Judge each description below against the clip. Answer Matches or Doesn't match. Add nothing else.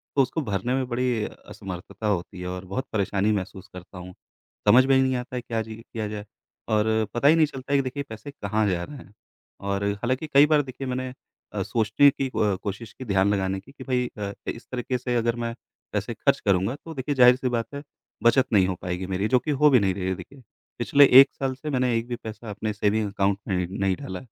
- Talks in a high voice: Doesn't match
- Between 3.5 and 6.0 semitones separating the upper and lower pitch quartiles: Matches